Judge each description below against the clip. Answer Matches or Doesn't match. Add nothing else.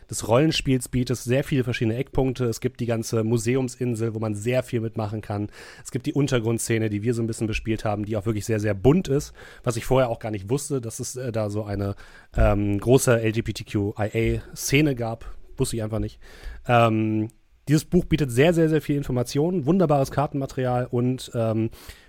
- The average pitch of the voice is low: Matches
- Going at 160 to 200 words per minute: Matches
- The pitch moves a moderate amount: Matches